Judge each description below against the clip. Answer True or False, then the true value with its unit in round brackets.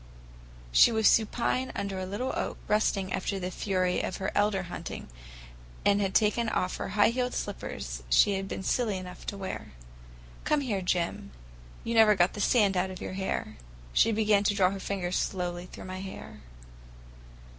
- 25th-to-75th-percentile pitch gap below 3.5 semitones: True (2.5 semitones)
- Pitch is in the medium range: False (195 Hz)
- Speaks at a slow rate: False (175 wpm)